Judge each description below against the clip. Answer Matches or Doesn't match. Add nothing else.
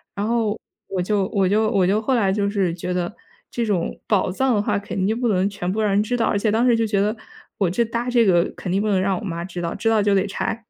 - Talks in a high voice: Matches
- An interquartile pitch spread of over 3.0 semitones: Doesn't match